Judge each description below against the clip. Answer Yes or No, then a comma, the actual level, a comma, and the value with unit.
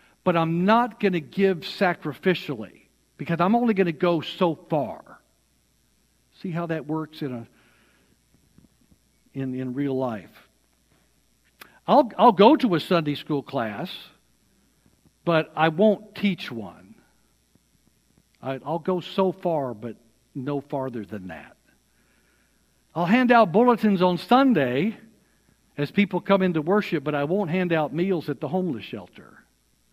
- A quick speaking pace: No, average, 140 wpm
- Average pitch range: No, wide, 6.3 semitones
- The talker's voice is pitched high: No, medium, 165 Hz